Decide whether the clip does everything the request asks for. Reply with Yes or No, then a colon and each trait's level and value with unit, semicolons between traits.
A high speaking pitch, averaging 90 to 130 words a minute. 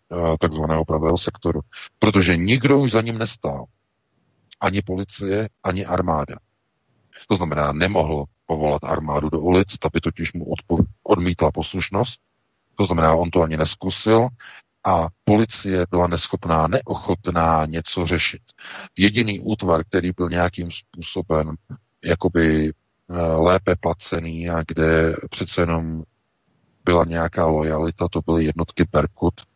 No: very low, 85 Hz; average, 120 wpm